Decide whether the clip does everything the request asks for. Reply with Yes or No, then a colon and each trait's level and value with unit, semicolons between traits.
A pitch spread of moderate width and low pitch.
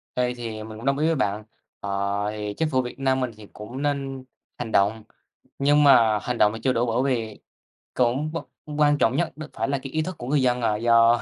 Yes: average, 3.9 semitones; low, 125 Hz